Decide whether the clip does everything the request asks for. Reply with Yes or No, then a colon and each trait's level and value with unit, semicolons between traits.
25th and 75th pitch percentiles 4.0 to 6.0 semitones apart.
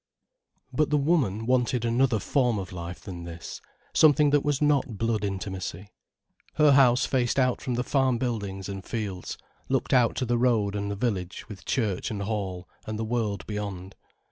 Yes: average, 4.6 semitones